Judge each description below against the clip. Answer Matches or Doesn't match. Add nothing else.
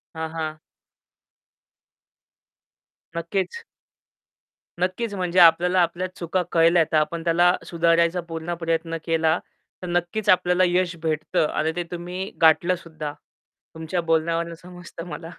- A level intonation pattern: Matches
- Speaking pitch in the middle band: Matches